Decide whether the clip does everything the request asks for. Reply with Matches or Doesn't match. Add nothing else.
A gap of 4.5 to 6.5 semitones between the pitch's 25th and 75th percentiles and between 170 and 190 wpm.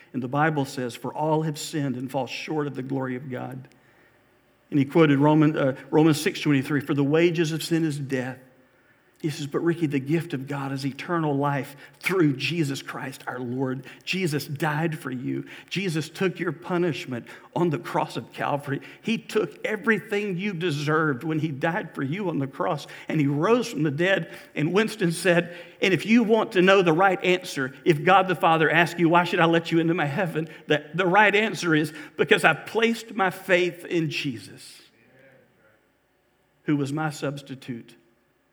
Doesn't match